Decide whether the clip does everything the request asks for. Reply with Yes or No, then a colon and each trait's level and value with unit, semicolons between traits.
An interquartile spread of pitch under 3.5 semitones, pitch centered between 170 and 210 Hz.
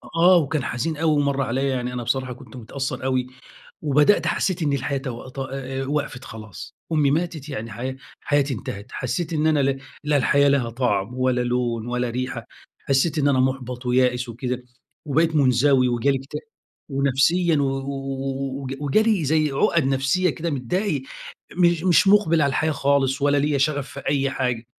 No: average, 2.8 semitones; low, 135 Hz